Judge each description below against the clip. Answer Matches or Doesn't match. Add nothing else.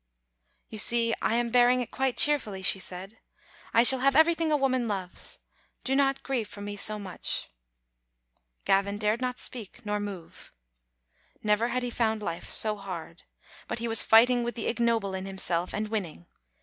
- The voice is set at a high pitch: Matches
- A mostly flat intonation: Doesn't match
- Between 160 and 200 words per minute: Matches